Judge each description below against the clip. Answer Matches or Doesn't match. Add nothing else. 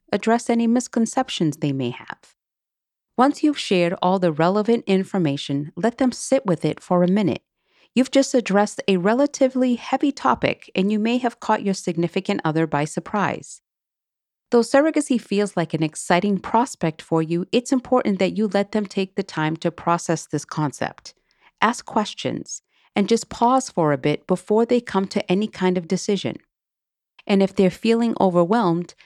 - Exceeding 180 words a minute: Doesn't match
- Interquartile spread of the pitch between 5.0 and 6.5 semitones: Matches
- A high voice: Matches